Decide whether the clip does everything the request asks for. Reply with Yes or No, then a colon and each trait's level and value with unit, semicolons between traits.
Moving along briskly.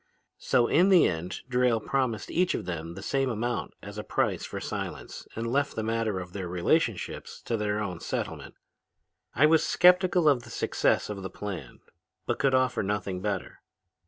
No: average, 180 wpm